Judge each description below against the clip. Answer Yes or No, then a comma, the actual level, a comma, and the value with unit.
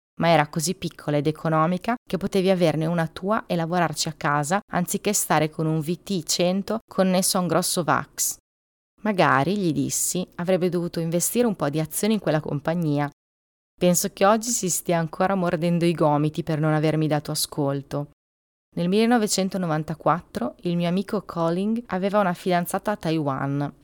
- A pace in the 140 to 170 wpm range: Yes, average, 160 wpm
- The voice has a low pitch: No, medium, 170 Hz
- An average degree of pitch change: Yes, average, 3.5 semitones